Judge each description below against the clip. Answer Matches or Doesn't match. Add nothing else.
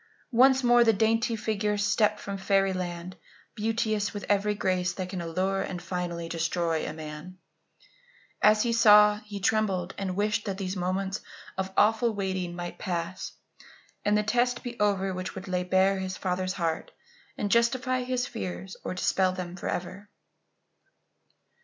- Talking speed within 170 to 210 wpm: Doesn't match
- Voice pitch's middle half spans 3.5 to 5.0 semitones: Doesn't match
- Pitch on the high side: Matches